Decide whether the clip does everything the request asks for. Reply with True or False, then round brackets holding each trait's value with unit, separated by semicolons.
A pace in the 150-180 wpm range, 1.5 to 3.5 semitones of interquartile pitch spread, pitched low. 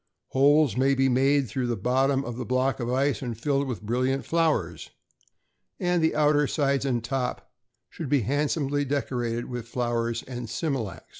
True (165 wpm; 2.9 semitones; 130 Hz)